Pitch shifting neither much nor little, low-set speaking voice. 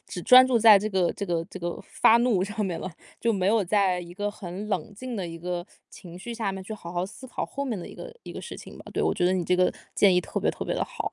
No: average, 3.7 semitones; high, 195 Hz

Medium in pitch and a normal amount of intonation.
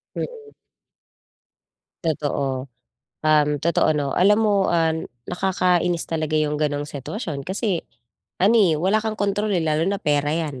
Yes: medium, 165 Hz; average, 4.7 semitones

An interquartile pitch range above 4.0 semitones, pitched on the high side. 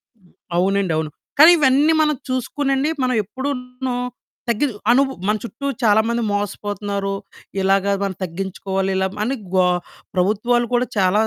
Yes: average, 5.0 semitones; high, 215 Hz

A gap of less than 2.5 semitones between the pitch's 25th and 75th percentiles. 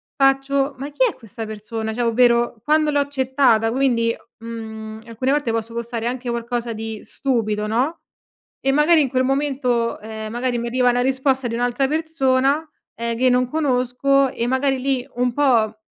No: average, 2.8 semitones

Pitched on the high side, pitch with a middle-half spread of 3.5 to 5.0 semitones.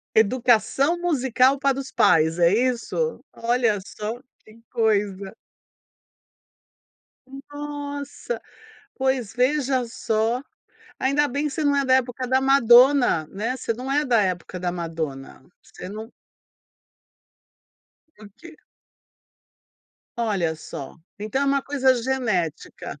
Yes: high, 245 Hz; average, 4.7 semitones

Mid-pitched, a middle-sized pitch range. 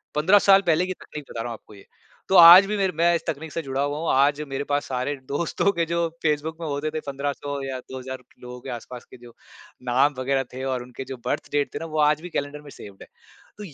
Yes: medium, 145 Hz; average, 3.8 semitones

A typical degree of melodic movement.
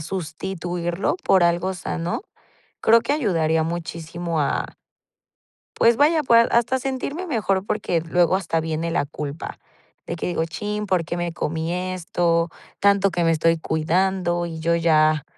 Yes: average, 3.2 semitones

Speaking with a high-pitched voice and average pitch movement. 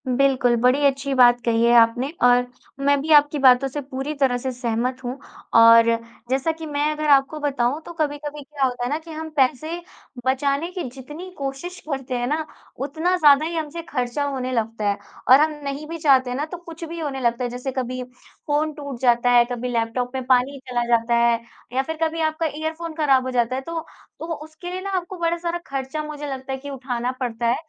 Yes: very high, 275 Hz; average, 3.8 semitones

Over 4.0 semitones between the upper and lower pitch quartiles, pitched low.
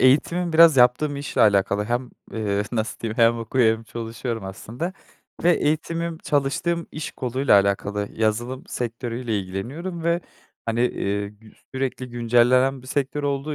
Yes: average, 4.4 semitones; low, 125 Hz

